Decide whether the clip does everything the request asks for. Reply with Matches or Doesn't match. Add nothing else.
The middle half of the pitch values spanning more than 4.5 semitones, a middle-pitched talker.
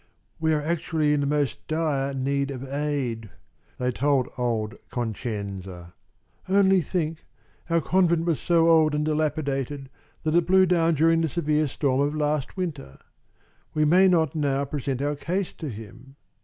Doesn't match